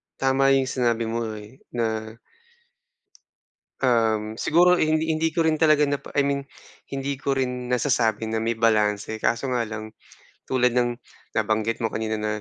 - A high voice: No, low, 120 Hz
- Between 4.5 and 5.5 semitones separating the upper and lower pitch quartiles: No, average, 3.7 semitones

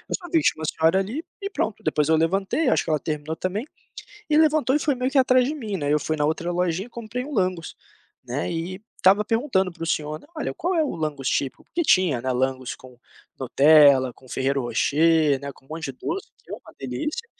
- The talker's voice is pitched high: No, medium, 170 Hz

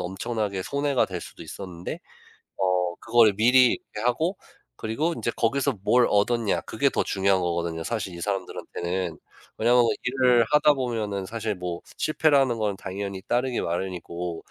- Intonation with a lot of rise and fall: No, average, 4.9 semitones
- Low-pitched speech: Yes, low, 105 Hz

